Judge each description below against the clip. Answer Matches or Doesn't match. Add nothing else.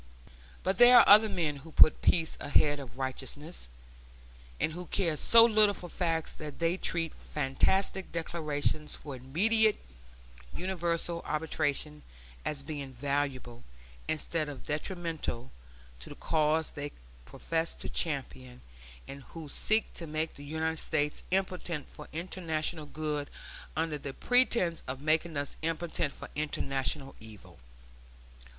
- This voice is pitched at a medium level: Matches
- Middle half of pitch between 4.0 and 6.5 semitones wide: Doesn't match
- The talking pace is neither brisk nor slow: Doesn't match